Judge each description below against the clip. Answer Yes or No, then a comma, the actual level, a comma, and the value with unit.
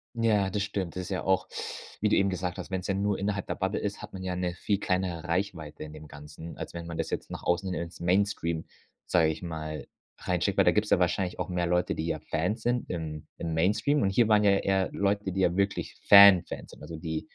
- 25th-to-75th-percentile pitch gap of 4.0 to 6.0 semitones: No, average, 2.9 semitones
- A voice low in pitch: Yes, very low, 90 Hz